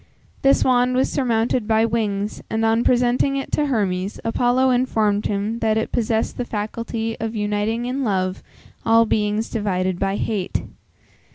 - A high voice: Yes, high, 225 Hz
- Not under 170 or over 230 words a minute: No, average, 155 wpm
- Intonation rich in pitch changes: No, average, 2.7 semitones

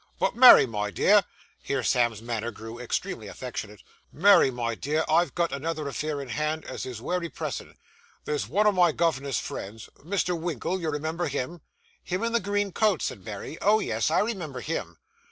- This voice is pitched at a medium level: Yes, medium, 155 Hz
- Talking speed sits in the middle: Yes, average, 180 wpm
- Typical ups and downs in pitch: No, wide, 6.3 semitones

